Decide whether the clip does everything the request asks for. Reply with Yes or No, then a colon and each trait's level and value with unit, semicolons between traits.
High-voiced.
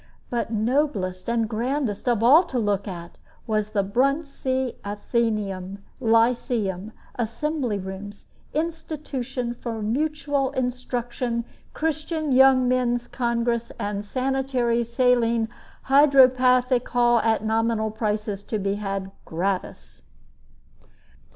Yes: high, 235 Hz